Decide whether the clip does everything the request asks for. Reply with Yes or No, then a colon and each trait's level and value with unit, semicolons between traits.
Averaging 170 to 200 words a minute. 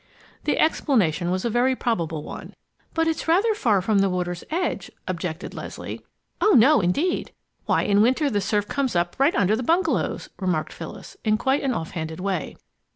Yes: average, 180 wpm